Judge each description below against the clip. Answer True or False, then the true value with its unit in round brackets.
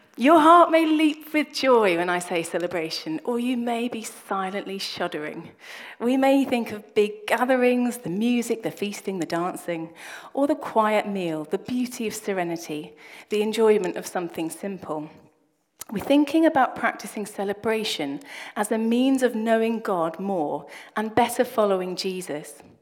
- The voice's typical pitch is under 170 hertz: False (210 Hz)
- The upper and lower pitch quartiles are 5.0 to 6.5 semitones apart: True (5.5 semitones)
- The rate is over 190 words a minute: False (150 wpm)